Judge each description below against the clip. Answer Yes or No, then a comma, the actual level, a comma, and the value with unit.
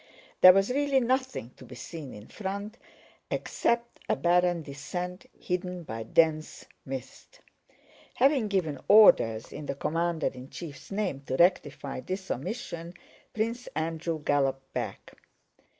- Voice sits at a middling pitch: Yes, medium, 175 Hz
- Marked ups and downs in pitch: Yes, wide, 6.1 semitones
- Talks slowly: Yes, slow, 130 wpm